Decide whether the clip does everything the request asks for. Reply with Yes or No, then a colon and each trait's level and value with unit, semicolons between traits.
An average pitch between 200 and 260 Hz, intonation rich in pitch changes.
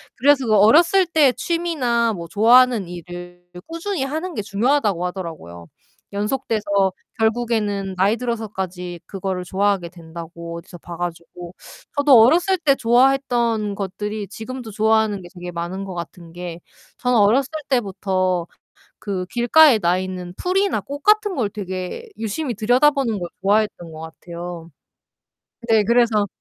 Yes: high, 210 Hz; wide, 5.7 semitones